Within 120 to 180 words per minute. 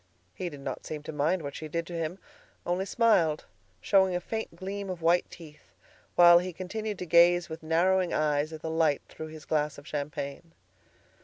No: average, 190 wpm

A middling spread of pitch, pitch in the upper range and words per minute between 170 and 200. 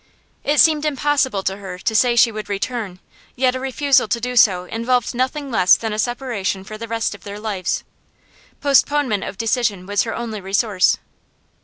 Yes: average, 4.1 semitones; high, 230 Hz; average, 175 wpm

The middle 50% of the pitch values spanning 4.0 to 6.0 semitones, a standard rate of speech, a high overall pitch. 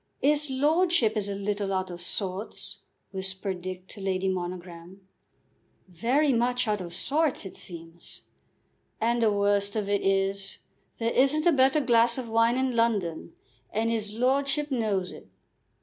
Yes: average, 4.8 semitones; average, 150 wpm; high, 210 Hz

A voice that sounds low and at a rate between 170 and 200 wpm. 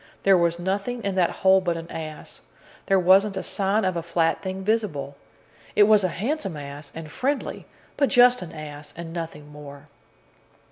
No: medium, 180 Hz; average, 180 wpm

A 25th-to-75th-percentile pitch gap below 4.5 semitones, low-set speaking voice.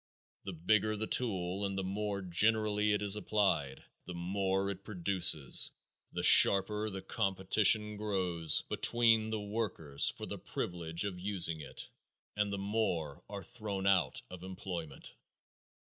Yes: average, 2.9 semitones; low, 100 Hz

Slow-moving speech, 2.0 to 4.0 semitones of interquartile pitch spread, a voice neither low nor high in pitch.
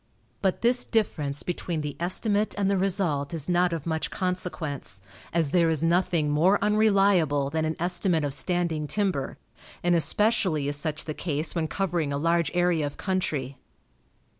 No: average, 165 wpm; average, 3.7 semitones; medium, 170 Hz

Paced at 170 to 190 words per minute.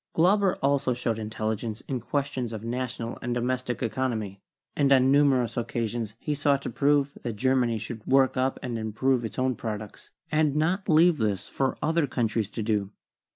Yes: average, 185 wpm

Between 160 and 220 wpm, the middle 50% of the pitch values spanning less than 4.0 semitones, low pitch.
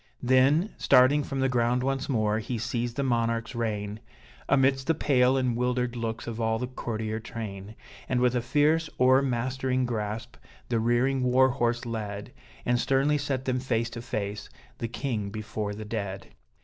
Yes: average, 165 wpm; average, 2.8 semitones; low, 120 Hz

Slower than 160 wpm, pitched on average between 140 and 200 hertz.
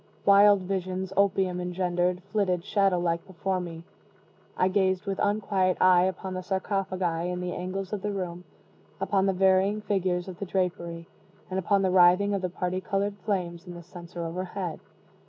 No: average, 170 wpm; medium, 185 Hz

